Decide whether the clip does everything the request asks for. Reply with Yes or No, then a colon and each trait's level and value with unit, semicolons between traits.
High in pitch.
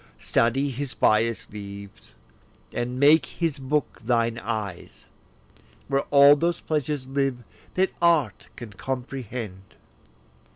No: low, 130 Hz